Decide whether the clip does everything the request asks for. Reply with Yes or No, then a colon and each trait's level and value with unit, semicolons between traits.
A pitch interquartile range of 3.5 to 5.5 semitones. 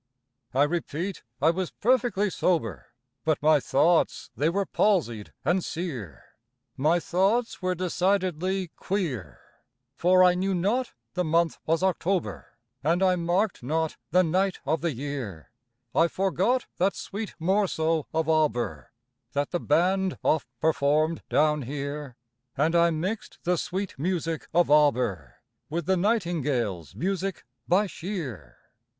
Yes: average, 4.0 semitones